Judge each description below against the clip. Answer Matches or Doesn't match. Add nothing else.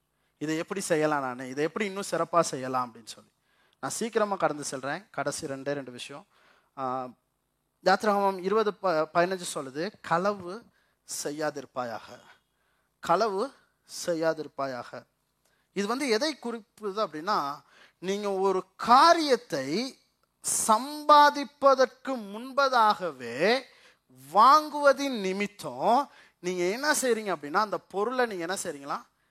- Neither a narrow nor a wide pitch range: Doesn't match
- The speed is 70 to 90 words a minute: Doesn't match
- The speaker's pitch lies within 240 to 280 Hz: Doesn't match